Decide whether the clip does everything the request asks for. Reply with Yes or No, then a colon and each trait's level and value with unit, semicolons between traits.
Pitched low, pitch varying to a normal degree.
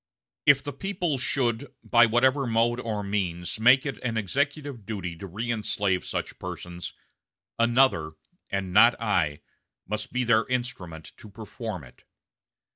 Yes: low, 115 Hz; average, 4.7 semitones